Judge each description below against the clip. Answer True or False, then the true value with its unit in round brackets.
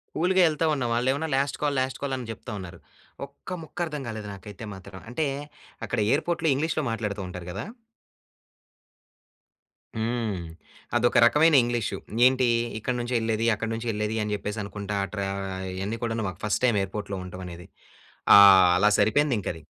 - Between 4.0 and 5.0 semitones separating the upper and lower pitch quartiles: True (4.7 semitones)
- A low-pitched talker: True (115 Hz)